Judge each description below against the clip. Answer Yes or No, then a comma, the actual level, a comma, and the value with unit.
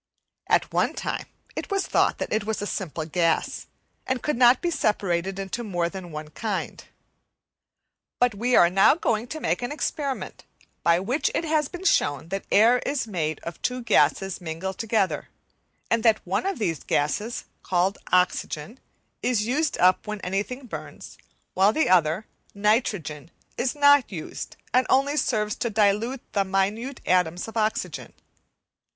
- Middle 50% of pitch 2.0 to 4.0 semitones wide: No, wide, 5.4 semitones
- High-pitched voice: Yes, high, 210 Hz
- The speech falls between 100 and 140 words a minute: No, average, 160 wpm